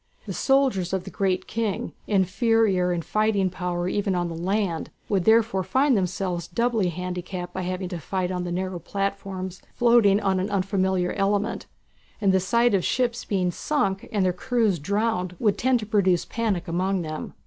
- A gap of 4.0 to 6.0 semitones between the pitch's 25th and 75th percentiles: No, average, 2.9 semitones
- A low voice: No, high, 190 Hz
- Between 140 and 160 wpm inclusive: No, average, 175 wpm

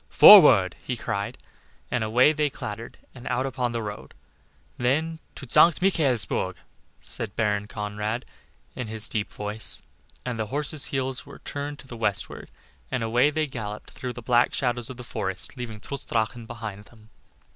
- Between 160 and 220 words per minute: Yes, average, 165 wpm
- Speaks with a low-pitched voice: Yes, low, 120 Hz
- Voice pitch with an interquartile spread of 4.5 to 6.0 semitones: No, average, 3.5 semitones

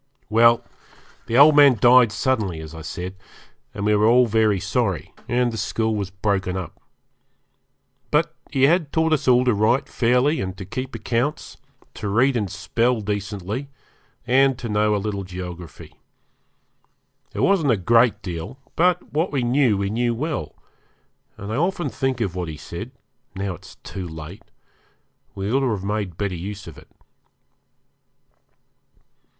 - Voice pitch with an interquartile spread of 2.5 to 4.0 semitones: No, average, 4.7 semitones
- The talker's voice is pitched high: No, low, 110 Hz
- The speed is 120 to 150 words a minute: No, average, 160 wpm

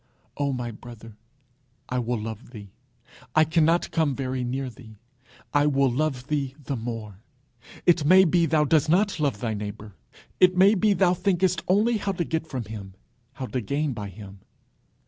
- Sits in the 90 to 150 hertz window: Yes, medium, 140 Hz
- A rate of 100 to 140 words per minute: No, average, 175 wpm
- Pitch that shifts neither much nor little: No, wide, 6.4 semitones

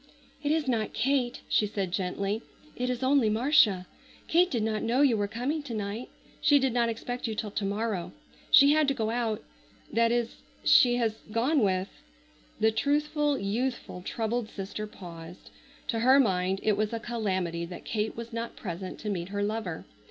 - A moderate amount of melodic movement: Yes, average, 3.8 semitones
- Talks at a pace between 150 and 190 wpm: Yes, average, 175 wpm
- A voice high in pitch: Yes, high, 225 Hz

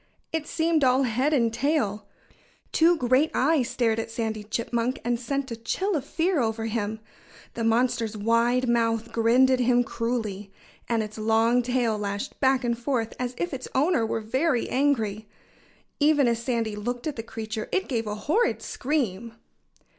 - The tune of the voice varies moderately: Yes, average, 3.0 semitones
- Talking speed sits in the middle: Yes, average, 170 wpm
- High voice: Yes, high, 235 Hz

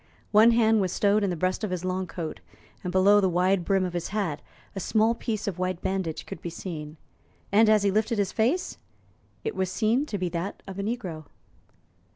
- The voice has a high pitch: Yes, high, 195 Hz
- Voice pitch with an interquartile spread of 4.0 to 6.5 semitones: No, average, 3.0 semitones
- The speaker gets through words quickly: Yes, fast, 210 wpm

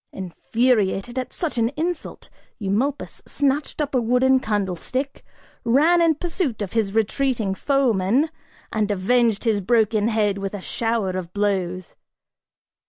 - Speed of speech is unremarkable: No, slow, 130 wpm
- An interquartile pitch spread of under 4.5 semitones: No, average, 4.9 semitones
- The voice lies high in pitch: Yes, high, 225 Hz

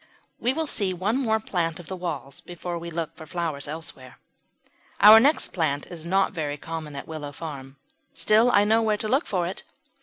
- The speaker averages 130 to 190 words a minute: No, average, 200 wpm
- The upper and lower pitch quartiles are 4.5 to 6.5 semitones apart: Yes, average, 5.1 semitones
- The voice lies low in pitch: No, medium, 170 Hz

